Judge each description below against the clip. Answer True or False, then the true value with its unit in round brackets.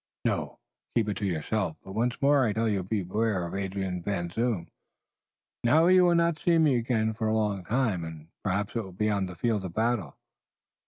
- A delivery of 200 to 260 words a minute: True (205 wpm)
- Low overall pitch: True (105 Hz)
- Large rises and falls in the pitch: False (4.0 semitones)